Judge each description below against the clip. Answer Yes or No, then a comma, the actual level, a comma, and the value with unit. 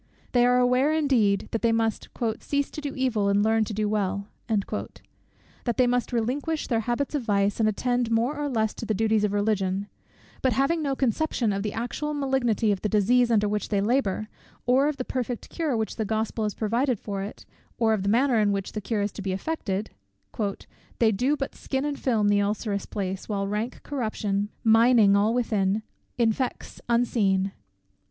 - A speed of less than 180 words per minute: No, average, 190 wpm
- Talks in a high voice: Yes, high, 225 Hz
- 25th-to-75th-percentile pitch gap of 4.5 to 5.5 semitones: No, average, 3.5 semitones